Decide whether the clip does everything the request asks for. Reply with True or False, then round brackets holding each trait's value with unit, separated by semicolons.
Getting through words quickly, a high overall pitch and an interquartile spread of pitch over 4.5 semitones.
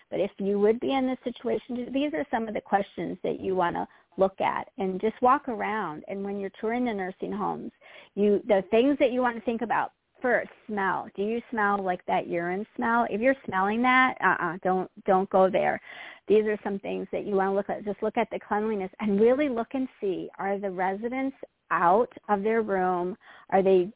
False (220 wpm; 210 Hz; 3.8 semitones)